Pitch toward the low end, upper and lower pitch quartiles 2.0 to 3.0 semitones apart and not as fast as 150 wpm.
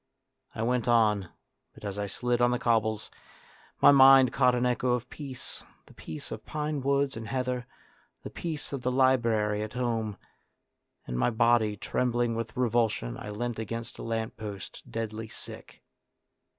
No: low, 120 Hz; average, 2.7 semitones; average, 165 wpm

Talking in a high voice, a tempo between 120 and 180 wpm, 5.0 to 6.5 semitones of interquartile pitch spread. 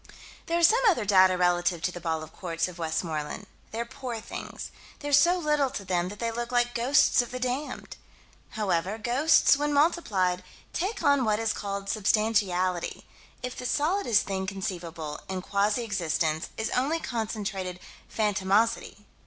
Yes: high, 210 Hz; average, 160 wpm; wide, 5.5 semitones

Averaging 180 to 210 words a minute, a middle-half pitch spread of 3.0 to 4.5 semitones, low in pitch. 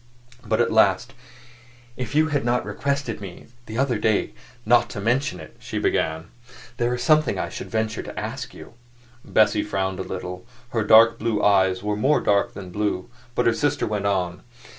Yes: average, 185 wpm; average, 3.9 semitones; low, 110 Hz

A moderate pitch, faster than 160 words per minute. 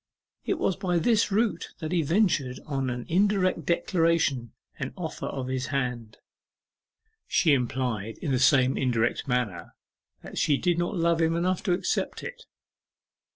No: medium, 155 Hz; average, 155 wpm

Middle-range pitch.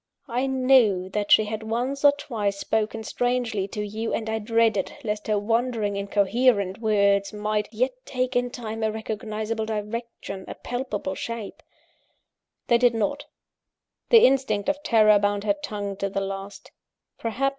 No: high, 220 Hz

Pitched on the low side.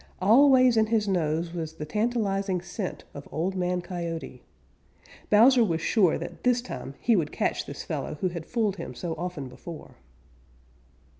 No: medium, 180 Hz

